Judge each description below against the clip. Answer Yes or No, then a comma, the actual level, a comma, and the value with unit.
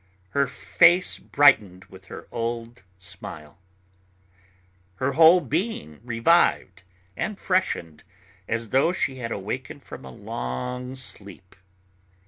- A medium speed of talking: No, slow, 110 wpm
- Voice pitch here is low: Yes, low, 115 Hz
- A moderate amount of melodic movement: No, wide, 6.7 semitones